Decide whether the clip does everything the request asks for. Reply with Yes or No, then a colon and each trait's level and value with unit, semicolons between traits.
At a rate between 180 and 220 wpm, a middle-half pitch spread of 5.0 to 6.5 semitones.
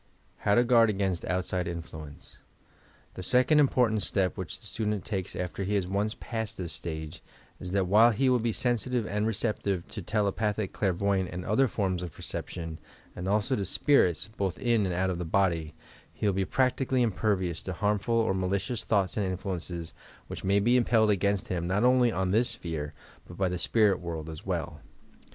No: average, 185 wpm; average, 3.6 semitones